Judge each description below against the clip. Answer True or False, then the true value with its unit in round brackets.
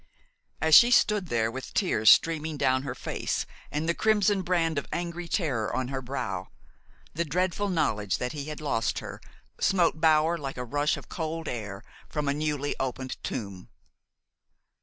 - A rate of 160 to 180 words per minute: True (165 wpm)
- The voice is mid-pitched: True (150 Hz)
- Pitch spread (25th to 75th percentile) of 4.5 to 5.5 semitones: True (4.8 semitones)